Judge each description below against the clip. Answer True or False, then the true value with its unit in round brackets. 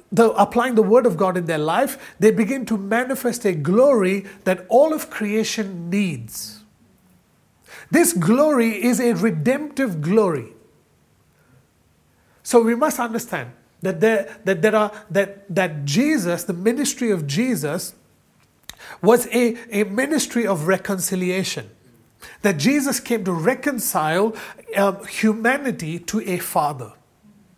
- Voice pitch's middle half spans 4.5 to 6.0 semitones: True (4.9 semitones)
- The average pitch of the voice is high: True (205 Hz)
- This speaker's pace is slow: True (125 wpm)